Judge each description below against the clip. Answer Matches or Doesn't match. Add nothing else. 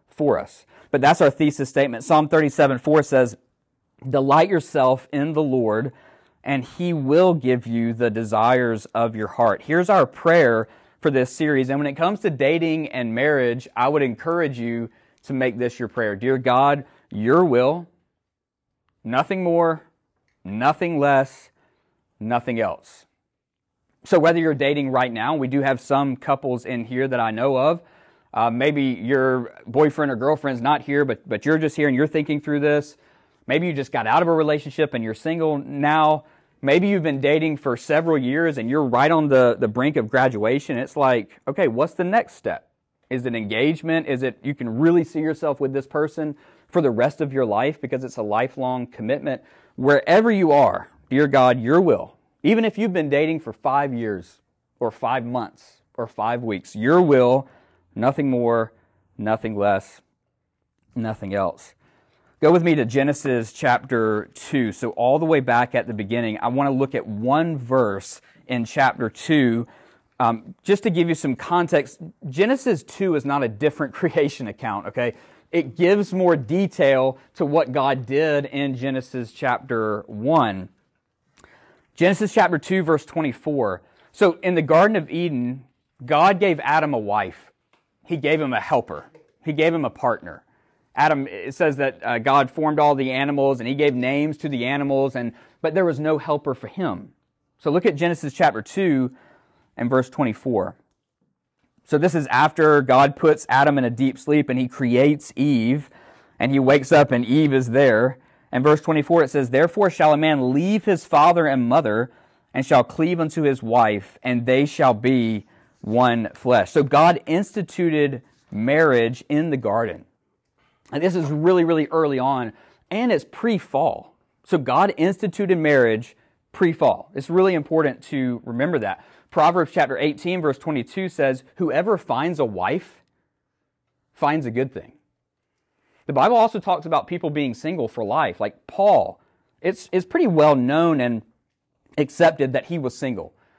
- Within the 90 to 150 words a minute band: Doesn't match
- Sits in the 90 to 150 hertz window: Matches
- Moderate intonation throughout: Matches